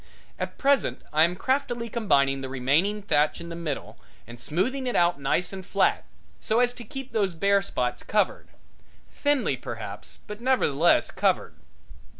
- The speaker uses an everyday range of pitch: No, wide, 8.0 semitones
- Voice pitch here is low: No, high, 195 Hz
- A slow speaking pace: No, average, 155 wpm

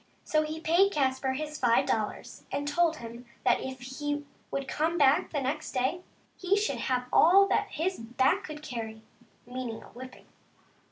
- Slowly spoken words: No, average, 175 wpm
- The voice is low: No, very high, 280 Hz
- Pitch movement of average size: Yes, average, 3.9 semitones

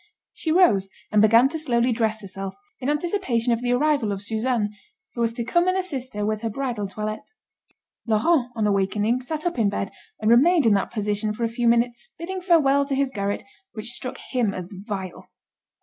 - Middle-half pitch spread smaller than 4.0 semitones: No, average, 4.6 semitones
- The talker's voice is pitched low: No, high, 235 Hz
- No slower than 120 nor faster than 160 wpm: No, average, 195 wpm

